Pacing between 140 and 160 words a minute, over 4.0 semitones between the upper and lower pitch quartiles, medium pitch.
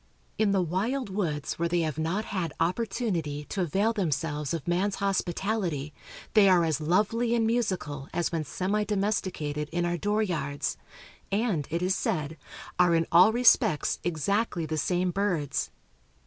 Yes: average, 155 wpm; average, 4.5 semitones; medium, 180 Hz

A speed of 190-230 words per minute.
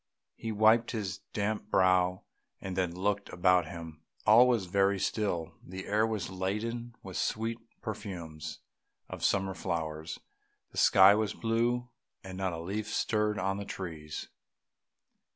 No: average, 145 wpm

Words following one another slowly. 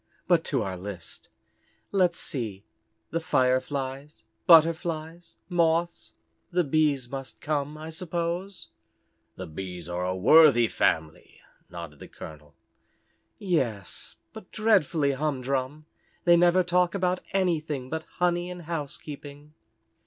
Yes: slow, 115 wpm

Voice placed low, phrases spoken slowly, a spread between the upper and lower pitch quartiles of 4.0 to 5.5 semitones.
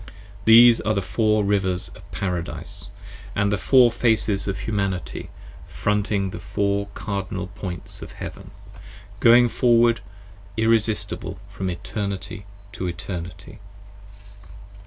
No: low, 100 Hz; slow, 115 wpm; average, 2.7 semitones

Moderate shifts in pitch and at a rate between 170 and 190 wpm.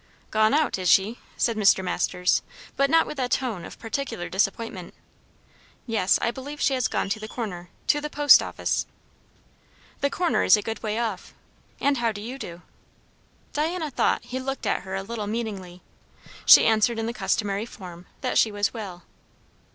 Yes: average, 5.0 semitones; average, 180 wpm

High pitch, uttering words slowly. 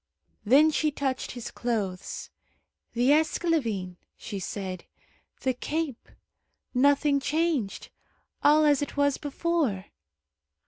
Yes: very high, 275 Hz; slow, 100 wpm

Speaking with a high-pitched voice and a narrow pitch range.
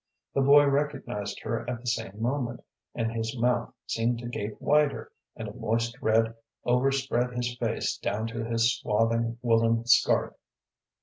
No: low, 115 Hz; narrow, 1.6 semitones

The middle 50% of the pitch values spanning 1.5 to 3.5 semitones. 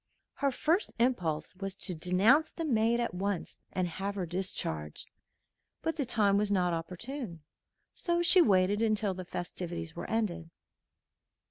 No: average, 5.0 semitones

